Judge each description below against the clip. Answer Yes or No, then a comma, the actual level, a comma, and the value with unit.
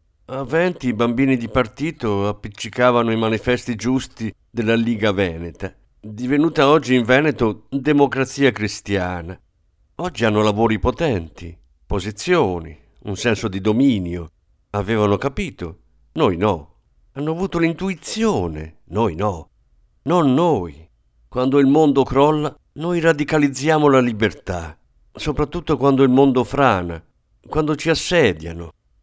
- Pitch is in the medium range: No, low, 115 Hz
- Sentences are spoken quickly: No, slow, 115 wpm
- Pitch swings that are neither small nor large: No, wide, 6.6 semitones